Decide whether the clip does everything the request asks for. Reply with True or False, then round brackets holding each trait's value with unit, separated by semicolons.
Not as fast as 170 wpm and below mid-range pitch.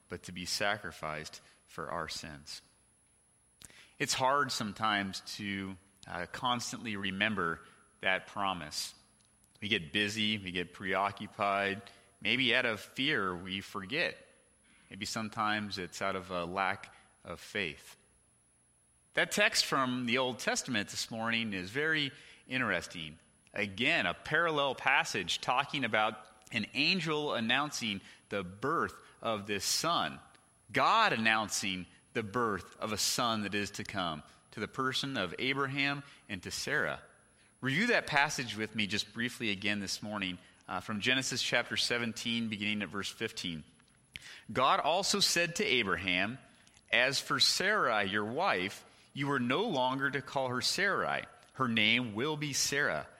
True (140 wpm; 105 Hz)